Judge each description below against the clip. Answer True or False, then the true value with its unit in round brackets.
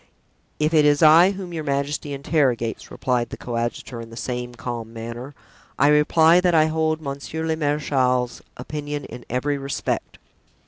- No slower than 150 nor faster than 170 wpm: True (155 wpm)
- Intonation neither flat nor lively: True (4.1 semitones)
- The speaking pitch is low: False (145 Hz)